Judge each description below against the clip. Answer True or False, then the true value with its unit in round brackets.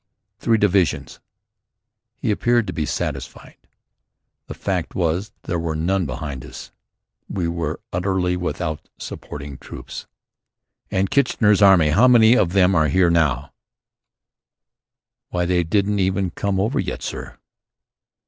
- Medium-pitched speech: False (90 Hz)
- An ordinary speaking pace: False (130 wpm)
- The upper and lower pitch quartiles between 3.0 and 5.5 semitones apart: True (3.4 semitones)